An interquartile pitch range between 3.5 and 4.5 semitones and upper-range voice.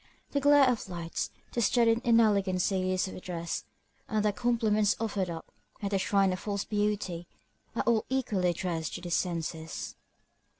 Yes: average, 3.8 semitones; high, 200 Hz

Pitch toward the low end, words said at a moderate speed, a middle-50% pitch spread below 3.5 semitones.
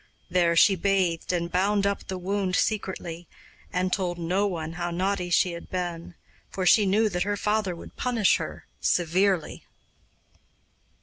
No: medium, 185 Hz; average, 150 wpm; narrow, 2.4 semitones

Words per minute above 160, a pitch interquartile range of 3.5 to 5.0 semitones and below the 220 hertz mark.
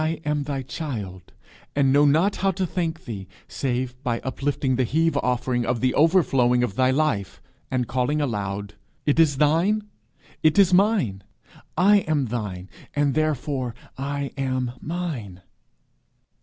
No: average, 145 wpm; average, 4.3 semitones; low, 135 Hz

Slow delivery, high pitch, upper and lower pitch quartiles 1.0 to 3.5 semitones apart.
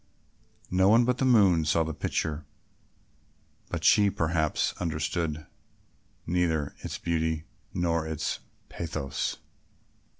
No: slow, 105 wpm; very low, 80 Hz; narrow, 2.4 semitones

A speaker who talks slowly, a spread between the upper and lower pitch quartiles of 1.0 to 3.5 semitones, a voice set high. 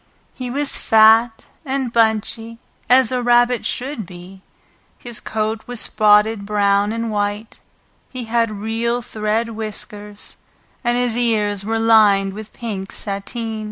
Yes: slow, 130 wpm; narrow, 2.4 semitones; high, 225 Hz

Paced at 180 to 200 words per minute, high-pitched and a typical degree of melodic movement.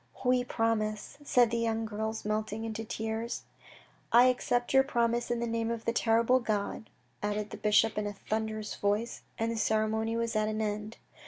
No: average, 190 wpm; high, 225 Hz; narrow, 1.5 semitones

